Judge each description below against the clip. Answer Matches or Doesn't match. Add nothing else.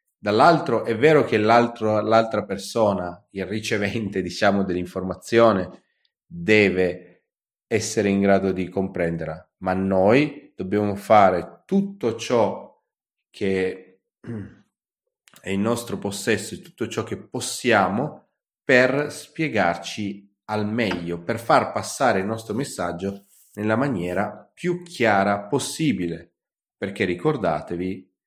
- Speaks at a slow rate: Matches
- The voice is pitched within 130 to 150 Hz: Doesn't match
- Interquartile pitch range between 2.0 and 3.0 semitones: Doesn't match